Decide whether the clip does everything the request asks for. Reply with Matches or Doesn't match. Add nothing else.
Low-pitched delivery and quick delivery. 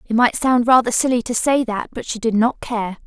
Doesn't match